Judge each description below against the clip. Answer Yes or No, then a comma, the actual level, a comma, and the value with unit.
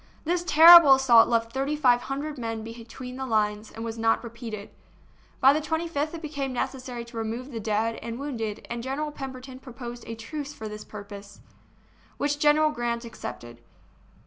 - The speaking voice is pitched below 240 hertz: No, high, 245 Hz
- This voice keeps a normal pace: Yes, average, 170 wpm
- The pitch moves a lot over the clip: No, average, 4.1 semitones